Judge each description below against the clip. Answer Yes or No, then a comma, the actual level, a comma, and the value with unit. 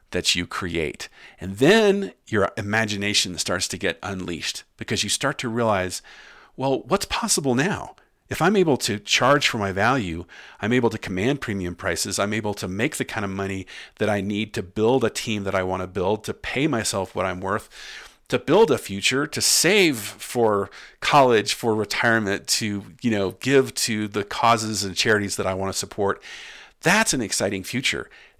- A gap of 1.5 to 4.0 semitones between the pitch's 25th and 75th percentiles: Yes, average, 3.0 semitones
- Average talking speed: Yes, average, 185 wpm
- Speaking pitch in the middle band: No, low, 105 Hz